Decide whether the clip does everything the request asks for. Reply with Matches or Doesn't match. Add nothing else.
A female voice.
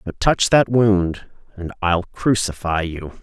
Doesn't match